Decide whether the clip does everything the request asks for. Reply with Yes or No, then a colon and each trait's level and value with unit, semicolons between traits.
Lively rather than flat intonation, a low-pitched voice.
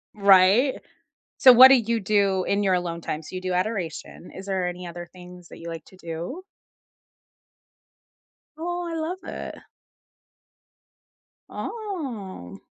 No: wide, 6.2 semitones; high, 190 Hz